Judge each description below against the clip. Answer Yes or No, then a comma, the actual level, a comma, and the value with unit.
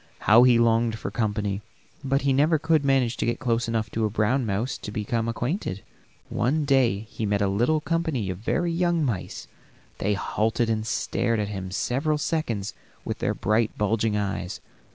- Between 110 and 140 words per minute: No, average, 180 wpm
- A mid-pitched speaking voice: No, low, 115 Hz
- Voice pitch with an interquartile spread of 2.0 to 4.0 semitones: No, average, 4.5 semitones